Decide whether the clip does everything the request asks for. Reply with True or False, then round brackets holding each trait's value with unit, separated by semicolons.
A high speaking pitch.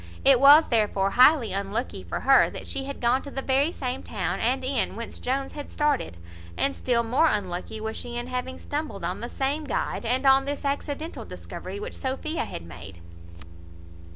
True (260 Hz)